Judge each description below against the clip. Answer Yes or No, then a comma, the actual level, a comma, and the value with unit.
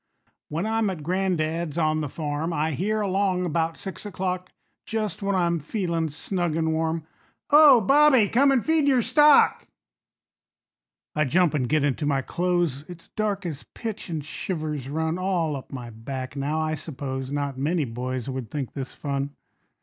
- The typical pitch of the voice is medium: Yes, medium, 160 Hz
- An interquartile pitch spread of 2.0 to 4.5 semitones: No, average, 4.9 semitones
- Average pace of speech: Yes, average, 165 wpm